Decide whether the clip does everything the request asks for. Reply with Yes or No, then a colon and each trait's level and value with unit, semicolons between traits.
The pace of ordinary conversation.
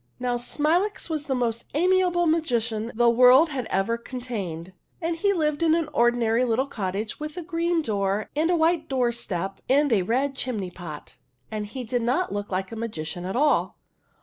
Yes: average, 180 wpm